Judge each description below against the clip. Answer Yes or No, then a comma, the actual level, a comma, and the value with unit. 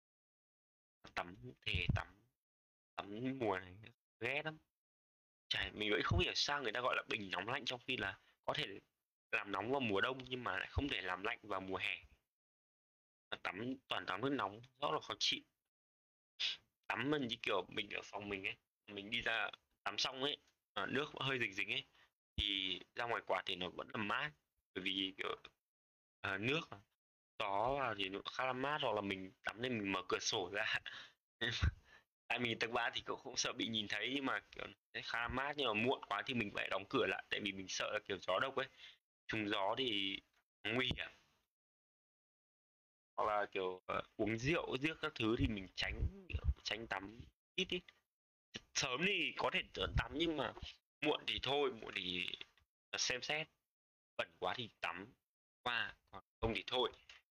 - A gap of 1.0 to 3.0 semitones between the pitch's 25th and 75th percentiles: No, wide, 5.6 semitones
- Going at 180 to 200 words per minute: Yes, average, 190 wpm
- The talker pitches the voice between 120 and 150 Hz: No, low, 100 Hz